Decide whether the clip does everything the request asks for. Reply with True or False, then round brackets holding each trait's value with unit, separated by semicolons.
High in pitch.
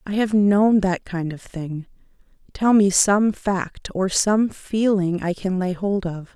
True (195 Hz)